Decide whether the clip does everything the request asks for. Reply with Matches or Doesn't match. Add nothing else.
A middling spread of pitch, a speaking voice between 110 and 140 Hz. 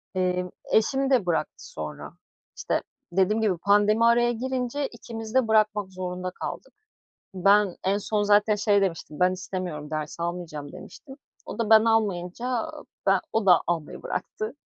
Doesn't match